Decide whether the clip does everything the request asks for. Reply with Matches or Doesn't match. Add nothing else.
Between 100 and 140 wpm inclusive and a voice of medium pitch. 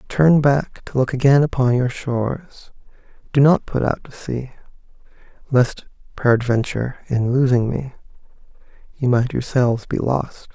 Doesn't match